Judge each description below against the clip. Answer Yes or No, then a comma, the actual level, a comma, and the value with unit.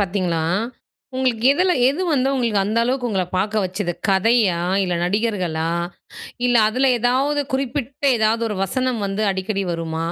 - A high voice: Yes, high, 215 Hz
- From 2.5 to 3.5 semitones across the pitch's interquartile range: No, average, 5.1 semitones